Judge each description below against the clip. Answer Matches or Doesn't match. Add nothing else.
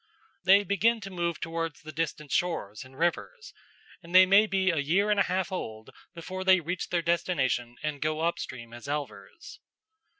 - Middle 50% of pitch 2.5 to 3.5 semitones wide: Doesn't match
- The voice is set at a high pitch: Doesn't match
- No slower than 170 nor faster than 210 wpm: Matches